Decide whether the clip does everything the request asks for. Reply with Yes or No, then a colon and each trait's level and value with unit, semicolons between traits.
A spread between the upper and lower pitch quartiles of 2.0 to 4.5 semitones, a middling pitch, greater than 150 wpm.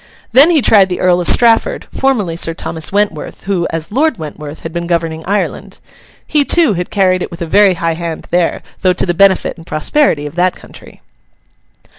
Yes: average, 3.9 semitones; medium, 180 Hz; average, 195 wpm